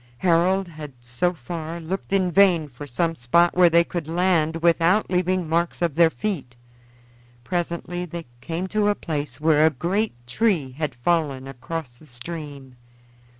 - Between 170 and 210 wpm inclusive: No, average, 155 wpm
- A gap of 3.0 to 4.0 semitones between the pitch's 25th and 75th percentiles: Yes, average, 3.3 semitones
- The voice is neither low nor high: Yes, medium, 165 Hz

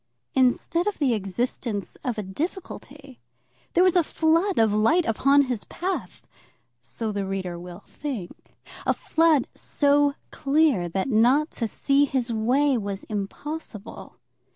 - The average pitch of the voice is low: No, very high, 255 Hz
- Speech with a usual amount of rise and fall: No, wide, 6.0 semitones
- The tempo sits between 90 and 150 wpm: Yes, slow, 135 wpm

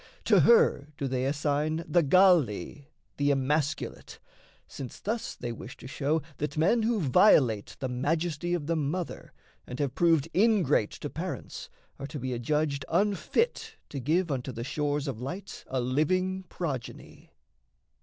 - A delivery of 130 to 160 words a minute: Yes, average, 150 wpm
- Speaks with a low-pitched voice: No, medium, 150 Hz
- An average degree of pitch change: Yes, average, 4.8 semitones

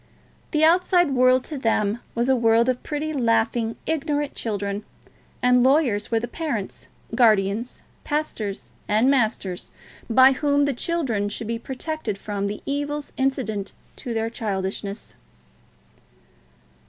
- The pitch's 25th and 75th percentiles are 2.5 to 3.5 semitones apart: No, average, 5.0 semitones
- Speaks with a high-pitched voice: Yes, high, 240 Hz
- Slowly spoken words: Yes, slow, 130 wpm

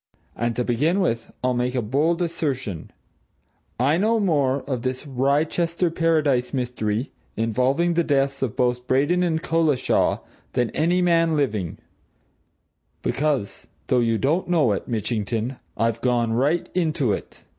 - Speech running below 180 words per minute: Yes, average, 140 wpm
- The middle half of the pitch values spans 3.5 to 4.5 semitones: No, average, 5.2 semitones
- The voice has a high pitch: No, low, 135 Hz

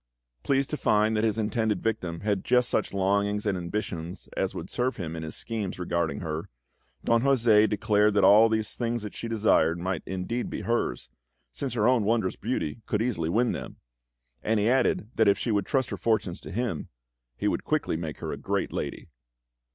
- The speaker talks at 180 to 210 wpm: Yes, average, 195 wpm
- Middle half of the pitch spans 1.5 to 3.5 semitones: No, average, 4.0 semitones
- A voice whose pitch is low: Yes, low, 105 Hz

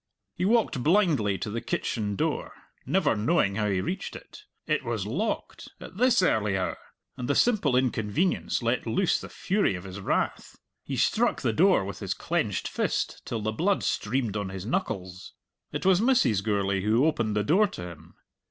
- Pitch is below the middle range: Yes, low, 115 Hz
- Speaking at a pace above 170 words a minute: Yes, average, 180 wpm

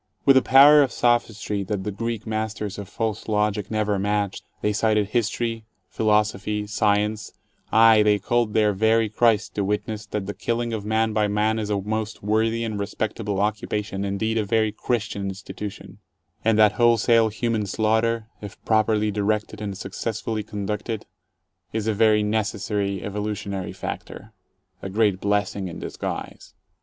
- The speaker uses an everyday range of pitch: No, narrow, 1.4 semitones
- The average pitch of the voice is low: Yes, low, 105 Hz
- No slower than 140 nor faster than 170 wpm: Yes, average, 155 wpm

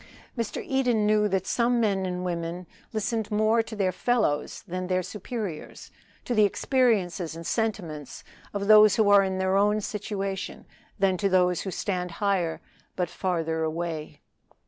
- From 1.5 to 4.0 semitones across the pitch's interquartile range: Yes, average, 3.1 semitones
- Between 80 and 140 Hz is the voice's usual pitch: No, high, 195 Hz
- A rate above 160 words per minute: No, average, 155 wpm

